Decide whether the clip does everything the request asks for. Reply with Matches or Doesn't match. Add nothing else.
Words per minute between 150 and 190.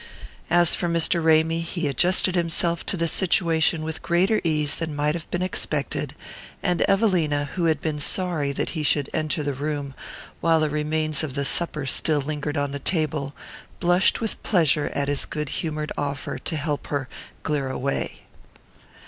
Matches